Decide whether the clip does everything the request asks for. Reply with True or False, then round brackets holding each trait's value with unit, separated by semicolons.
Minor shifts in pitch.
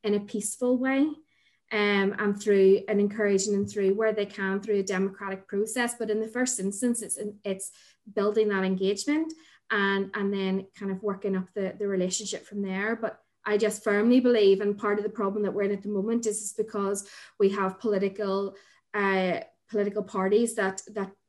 True (1.5 semitones)